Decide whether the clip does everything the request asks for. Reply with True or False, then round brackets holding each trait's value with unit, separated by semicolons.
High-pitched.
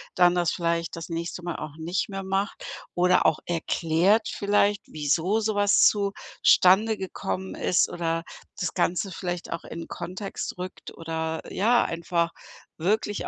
False (180 Hz)